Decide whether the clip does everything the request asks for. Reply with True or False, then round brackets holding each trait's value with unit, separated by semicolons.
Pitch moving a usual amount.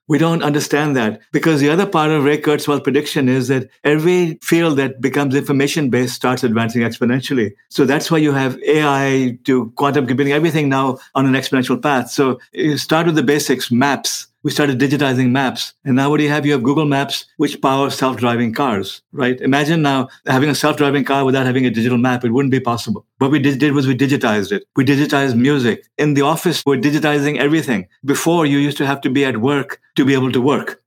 False (2.1 semitones)